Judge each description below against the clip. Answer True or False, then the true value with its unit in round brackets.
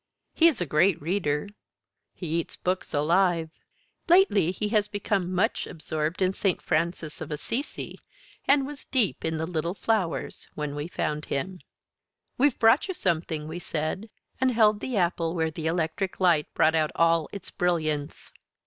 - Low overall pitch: False (175 Hz)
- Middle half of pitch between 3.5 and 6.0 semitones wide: True (4.4 semitones)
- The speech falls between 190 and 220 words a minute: False (160 wpm)